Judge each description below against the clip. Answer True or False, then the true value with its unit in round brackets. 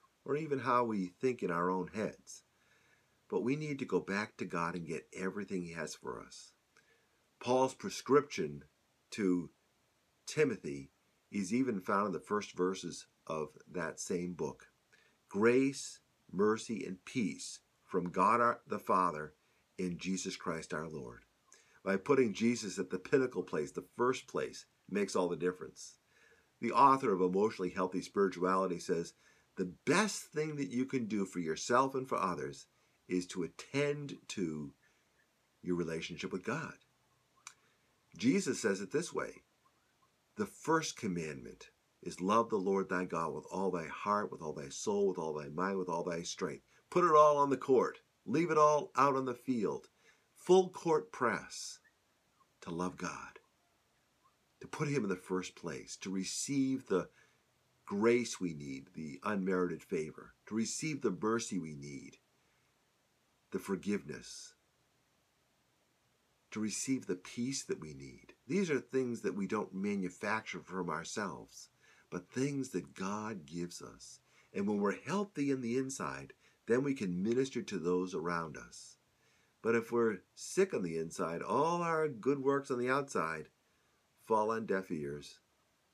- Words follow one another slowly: False (155 wpm)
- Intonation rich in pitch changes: True (6.7 semitones)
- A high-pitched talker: False (105 Hz)